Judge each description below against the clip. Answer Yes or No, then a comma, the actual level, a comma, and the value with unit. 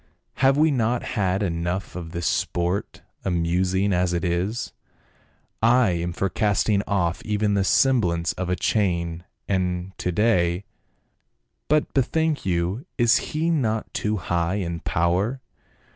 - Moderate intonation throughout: Yes, average, 4.3 semitones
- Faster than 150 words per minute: No, average, 145 wpm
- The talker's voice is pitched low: Yes, very low, 95 Hz